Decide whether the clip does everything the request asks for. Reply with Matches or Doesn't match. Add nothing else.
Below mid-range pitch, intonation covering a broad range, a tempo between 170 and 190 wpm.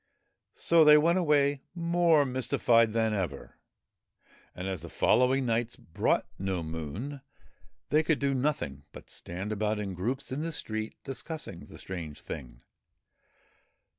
Doesn't match